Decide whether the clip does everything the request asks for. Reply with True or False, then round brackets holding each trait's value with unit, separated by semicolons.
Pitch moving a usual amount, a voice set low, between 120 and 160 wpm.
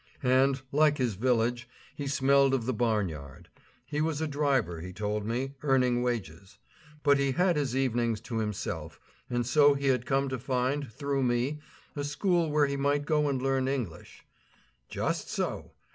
False (3.3 semitones; 130 Hz; 175 wpm)